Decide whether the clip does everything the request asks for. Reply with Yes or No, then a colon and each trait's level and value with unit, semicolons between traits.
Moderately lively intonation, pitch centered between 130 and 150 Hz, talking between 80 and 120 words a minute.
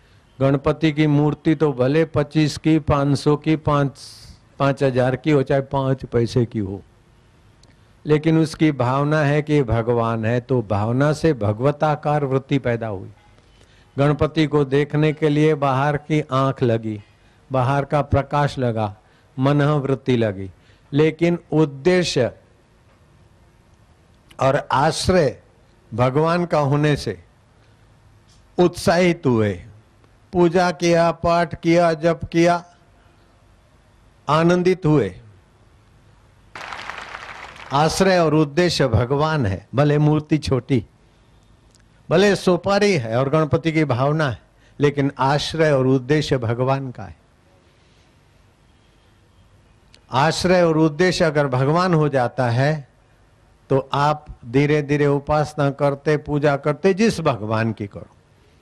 Yes: average, 5.0 semitones; low, 135 Hz; average, 115 wpm